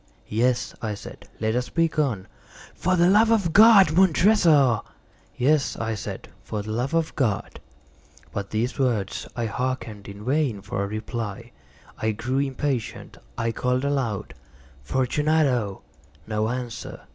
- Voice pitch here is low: Yes, low, 125 Hz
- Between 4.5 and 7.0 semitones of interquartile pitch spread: Yes, wide, 5.5 semitones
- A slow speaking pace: No, average, 145 wpm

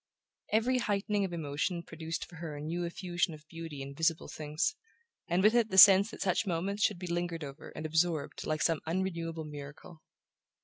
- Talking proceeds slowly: No, average, 185 wpm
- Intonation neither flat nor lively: Yes, average, 3.3 semitones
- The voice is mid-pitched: Yes, medium, 170 Hz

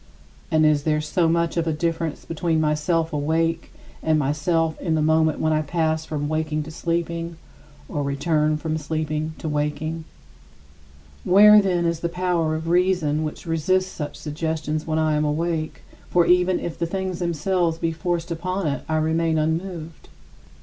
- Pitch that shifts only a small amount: Yes, narrow, 1.7 semitones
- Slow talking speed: No, average, 165 wpm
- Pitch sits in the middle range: Yes, medium, 160 Hz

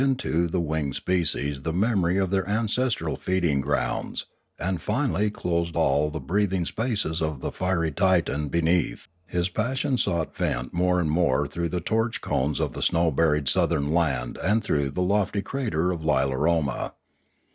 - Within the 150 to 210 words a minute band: Yes, average, 165 wpm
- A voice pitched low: Yes, very low, 85 Hz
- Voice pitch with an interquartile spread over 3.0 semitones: Yes, average, 4.3 semitones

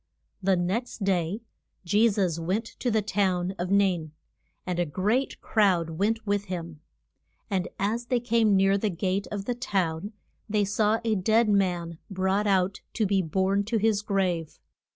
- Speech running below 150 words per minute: No, average, 165 wpm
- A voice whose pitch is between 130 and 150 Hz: No, high, 195 Hz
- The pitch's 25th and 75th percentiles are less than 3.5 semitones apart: Yes, average, 2.8 semitones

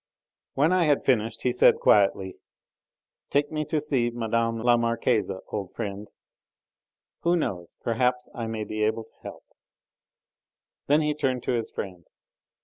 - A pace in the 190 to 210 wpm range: No, average, 145 wpm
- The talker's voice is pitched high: No, low, 120 Hz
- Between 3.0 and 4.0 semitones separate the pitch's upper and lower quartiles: No, average, 4.7 semitones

